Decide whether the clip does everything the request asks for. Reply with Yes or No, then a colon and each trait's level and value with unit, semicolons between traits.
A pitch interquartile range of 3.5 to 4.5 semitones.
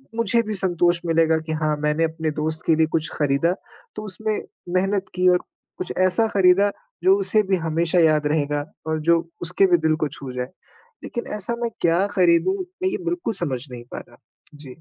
Yes: average, 3.9 semitones